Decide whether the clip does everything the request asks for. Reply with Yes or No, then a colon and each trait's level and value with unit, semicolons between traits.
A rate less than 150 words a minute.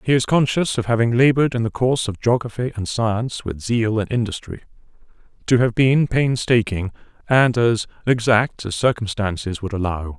No: average, 165 wpm